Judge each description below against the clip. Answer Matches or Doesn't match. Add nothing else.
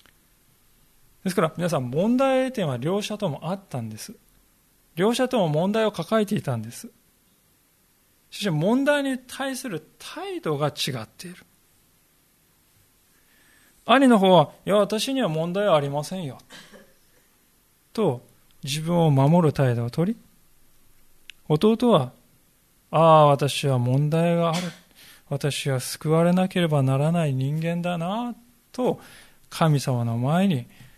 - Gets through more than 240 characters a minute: Doesn't match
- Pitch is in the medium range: Matches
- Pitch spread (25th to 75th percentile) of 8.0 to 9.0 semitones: Doesn't match